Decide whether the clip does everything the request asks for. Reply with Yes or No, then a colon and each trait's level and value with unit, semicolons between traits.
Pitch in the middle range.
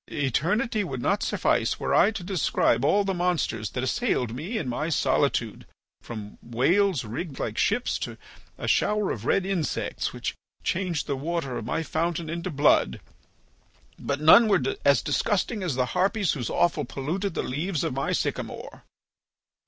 Yes: medium, 165 Hz